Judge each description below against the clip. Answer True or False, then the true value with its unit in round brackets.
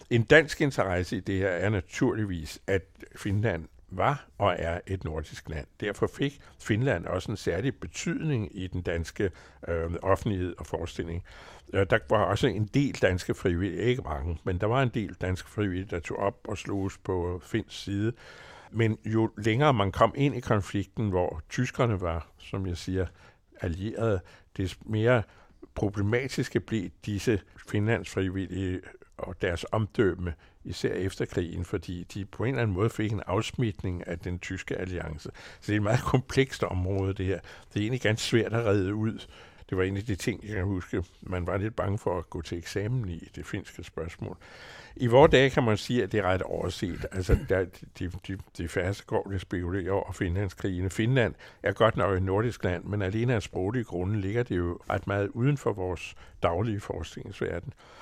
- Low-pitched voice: True (100 Hz)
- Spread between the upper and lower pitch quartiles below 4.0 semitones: True (3.6 semitones)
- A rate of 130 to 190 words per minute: True (185 wpm)